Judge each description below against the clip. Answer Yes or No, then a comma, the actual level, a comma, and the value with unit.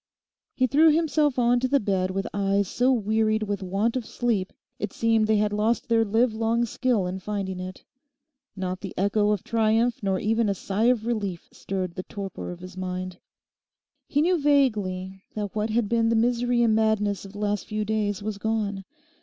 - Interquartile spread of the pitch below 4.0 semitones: Yes, average, 3.1 semitones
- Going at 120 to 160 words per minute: No, average, 190 wpm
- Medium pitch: No, high, 215 Hz